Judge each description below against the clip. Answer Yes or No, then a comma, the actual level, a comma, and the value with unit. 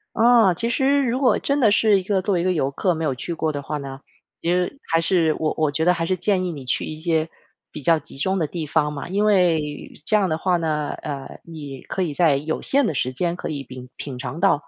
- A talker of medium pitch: Yes, medium, 165 Hz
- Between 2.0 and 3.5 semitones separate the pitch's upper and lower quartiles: No, average, 4.2 semitones